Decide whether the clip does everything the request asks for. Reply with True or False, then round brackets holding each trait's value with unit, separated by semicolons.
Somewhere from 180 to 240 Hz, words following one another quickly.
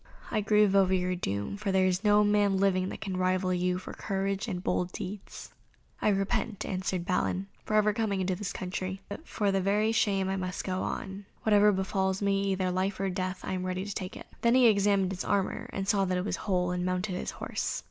True (190 Hz; 225 wpm)